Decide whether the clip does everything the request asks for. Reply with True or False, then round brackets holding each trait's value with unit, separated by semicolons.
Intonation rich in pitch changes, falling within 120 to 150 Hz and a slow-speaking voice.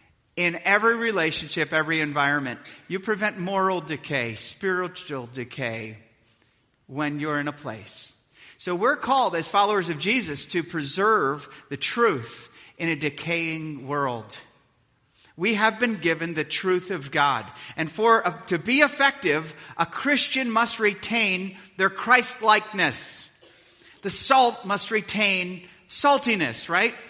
False (6.7 semitones; 170 Hz; 130 wpm)